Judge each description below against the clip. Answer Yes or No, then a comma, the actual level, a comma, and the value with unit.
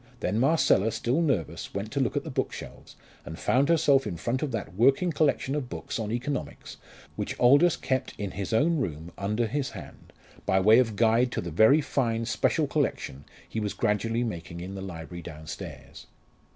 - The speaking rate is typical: Yes, average, 185 wpm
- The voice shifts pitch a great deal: Yes, wide, 6.2 semitones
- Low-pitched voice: Yes, low, 115 Hz